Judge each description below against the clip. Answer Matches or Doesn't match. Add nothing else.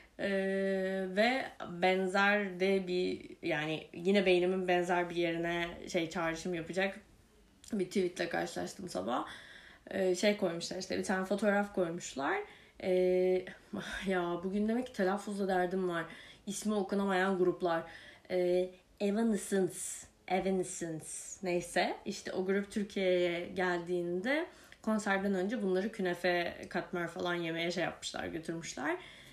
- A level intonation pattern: Matches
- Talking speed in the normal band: Matches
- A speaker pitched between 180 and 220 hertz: Matches